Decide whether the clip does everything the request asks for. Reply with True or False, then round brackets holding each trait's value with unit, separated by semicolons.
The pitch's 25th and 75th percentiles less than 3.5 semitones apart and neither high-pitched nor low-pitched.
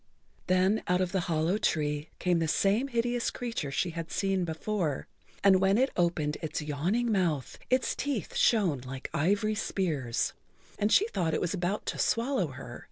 False (5.3 semitones; 180 Hz)